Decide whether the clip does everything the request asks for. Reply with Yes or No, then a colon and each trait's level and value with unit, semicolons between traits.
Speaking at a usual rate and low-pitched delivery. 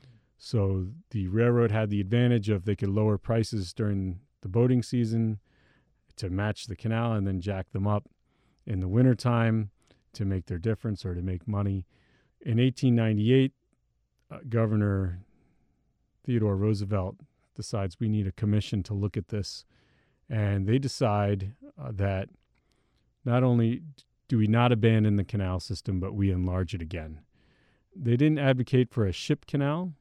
Yes: average, 155 wpm; low, 110 Hz